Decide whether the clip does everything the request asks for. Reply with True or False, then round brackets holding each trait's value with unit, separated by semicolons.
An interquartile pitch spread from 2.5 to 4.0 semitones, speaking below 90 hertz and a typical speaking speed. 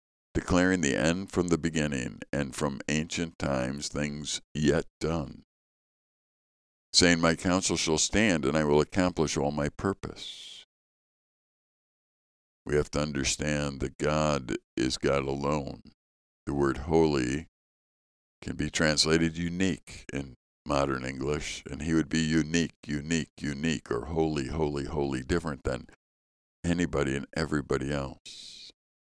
False (2.8 semitones; 75 Hz; 125 wpm)